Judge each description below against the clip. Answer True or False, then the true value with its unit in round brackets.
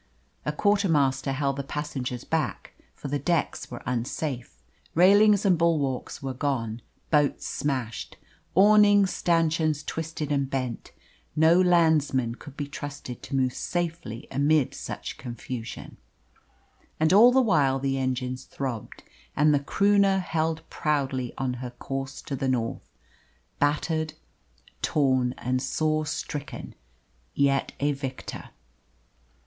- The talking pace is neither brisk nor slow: False (125 wpm)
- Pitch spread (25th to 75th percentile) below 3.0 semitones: False (3.8 semitones)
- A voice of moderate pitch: True (145 Hz)